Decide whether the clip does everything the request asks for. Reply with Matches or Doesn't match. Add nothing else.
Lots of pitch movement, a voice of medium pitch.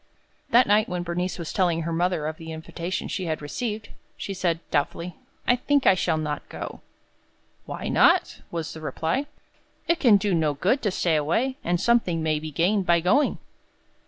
Doesn't match